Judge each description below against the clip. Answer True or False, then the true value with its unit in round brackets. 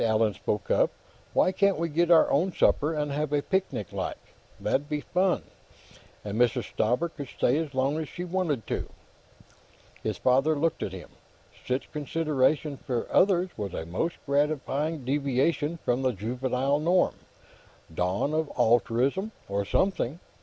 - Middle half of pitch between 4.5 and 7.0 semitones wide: True (4.9 semitones)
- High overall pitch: False (145 Hz)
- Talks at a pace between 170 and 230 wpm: False (155 wpm)